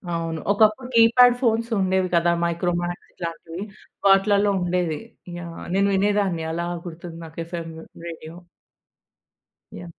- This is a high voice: No, medium, 180 Hz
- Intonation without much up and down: No, average, 3.3 semitones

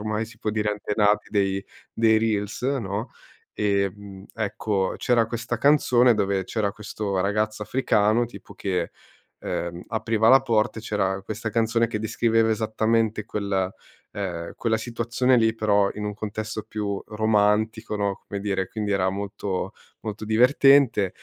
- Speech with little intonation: Yes, narrow, 1.9 semitones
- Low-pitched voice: Yes, low, 105 Hz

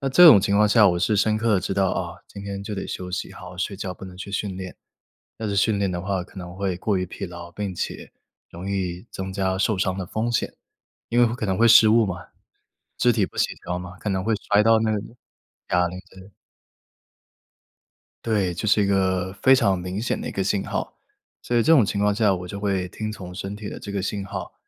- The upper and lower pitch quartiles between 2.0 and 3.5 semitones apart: Yes, narrow, 2.5 semitones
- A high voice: No, low, 100 Hz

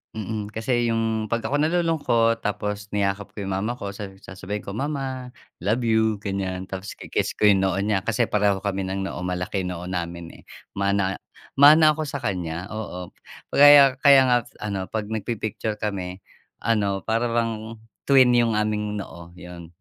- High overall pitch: No, low, 105 Hz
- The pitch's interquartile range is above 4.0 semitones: No, average, 3.3 semitones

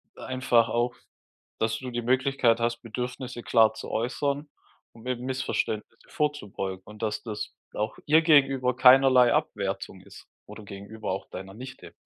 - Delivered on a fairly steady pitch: No, average, 3.2 semitones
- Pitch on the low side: Yes, low, 120 Hz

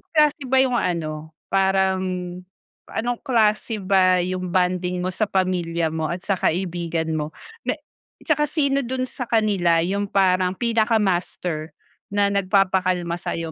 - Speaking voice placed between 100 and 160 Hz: No, medium, 185 Hz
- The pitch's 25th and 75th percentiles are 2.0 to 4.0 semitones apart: Yes, average, 3.7 semitones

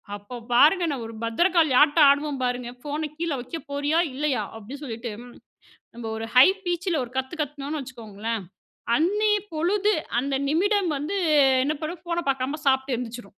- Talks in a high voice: Yes, very high, 285 Hz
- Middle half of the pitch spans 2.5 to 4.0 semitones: No, average, 5.0 semitones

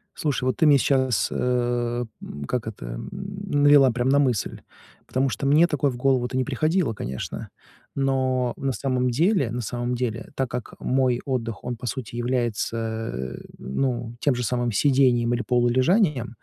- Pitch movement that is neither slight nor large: No, narrow, 2.3 semitones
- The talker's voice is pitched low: Yes, low, 125 Hz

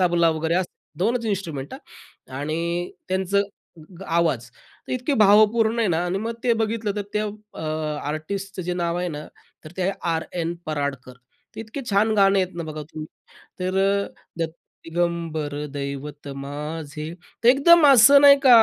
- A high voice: No, medium, 175 Hz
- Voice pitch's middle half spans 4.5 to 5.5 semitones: Yes, average, 5.2 semitones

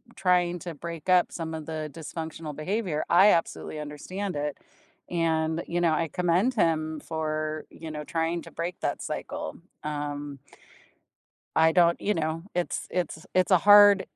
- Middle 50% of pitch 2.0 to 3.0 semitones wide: Yes, narrow, 2.4 semitones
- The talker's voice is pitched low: No, medium, 165 Hz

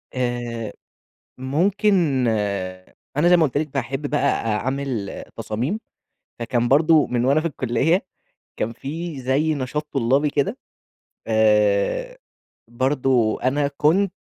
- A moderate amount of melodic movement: Yes, average, 4.4 semitones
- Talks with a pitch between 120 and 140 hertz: Yes, low, 135 Hz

